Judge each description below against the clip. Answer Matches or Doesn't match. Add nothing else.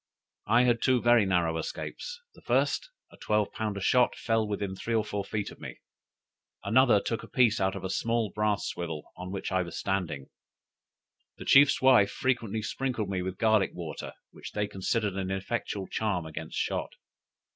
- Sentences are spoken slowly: Doesn't match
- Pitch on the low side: Matches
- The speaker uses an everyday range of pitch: Matches